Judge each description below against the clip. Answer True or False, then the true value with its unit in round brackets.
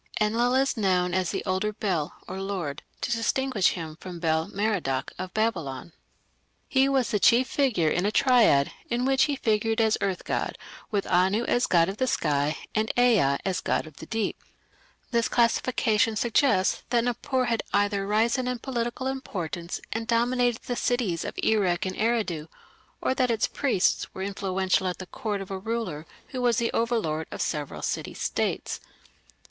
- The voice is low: False (210 Hz)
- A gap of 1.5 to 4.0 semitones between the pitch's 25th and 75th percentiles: False (4.8 semitones)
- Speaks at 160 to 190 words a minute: True (170 wpm)